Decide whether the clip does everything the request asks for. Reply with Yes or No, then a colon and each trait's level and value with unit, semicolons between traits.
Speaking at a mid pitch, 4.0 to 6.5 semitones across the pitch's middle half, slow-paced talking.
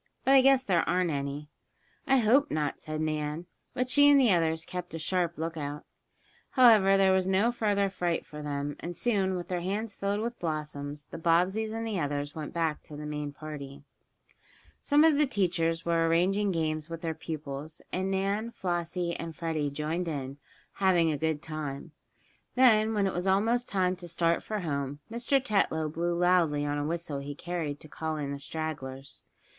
No: medium, 170 Hz; average, 4.5 semitones; average, 185 wpm